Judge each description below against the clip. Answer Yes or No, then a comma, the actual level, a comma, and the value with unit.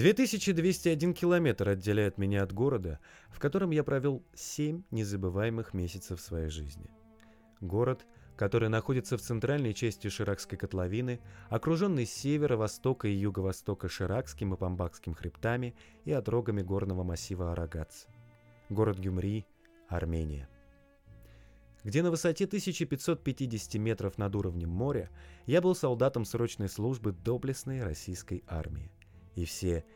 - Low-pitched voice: Yes, low, 110 Hz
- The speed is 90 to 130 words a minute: Yes, average, 115 wpm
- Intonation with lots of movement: Yes, wide, 5.7 semitones